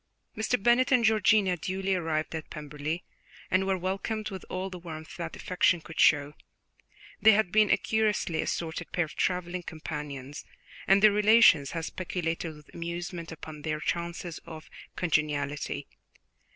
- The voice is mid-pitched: Yes, medium, 175 Hz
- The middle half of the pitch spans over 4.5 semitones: No, average, 3.5 semitones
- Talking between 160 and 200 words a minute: No, average, 150 wpm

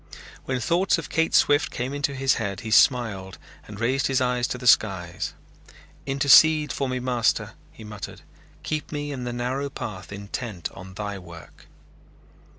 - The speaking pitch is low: Yes, low, 125 Hz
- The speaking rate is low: No, average, 160 wpm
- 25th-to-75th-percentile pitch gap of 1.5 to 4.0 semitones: No, average, 5.2 semitones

